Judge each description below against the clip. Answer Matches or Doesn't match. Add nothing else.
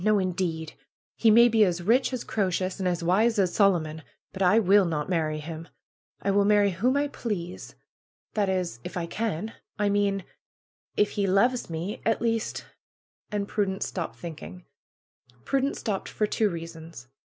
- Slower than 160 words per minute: Doesn't match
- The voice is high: Matches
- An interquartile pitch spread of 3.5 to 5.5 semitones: Matches